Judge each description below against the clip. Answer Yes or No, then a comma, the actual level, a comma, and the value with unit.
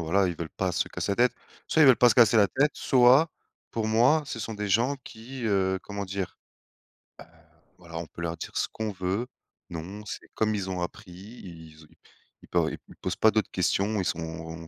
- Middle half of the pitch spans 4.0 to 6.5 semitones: Yes, average, 4.4 semitones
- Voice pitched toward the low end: Yes, low, 100 Hz